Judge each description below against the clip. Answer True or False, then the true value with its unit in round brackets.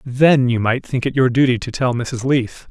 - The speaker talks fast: True (245 wpm)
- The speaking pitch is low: True (125 Hz)